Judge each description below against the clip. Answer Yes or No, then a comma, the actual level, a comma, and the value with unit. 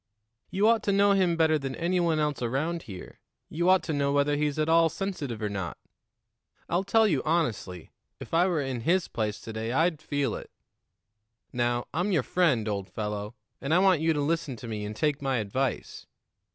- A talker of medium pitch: Yes, medium, 150 Hz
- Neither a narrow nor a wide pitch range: No, wide, 6.2 semitones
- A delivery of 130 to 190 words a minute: No, fast, 205 wpm